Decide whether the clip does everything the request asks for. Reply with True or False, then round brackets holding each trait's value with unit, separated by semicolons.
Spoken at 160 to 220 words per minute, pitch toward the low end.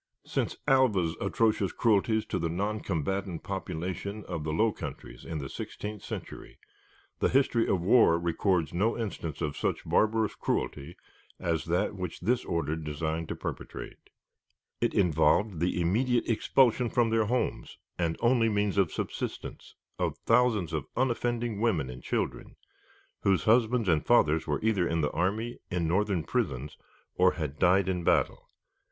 False (150 wpm; 95 Hz)